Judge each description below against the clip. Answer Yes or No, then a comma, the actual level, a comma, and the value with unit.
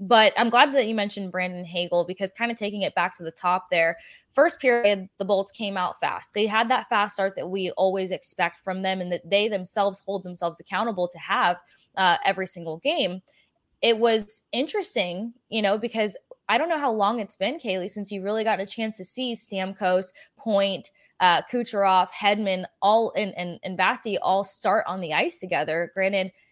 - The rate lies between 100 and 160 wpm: No, average, 200 wpm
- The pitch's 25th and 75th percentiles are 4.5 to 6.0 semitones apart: No, average, 3.1 semitones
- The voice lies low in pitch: No, high, 195 Hz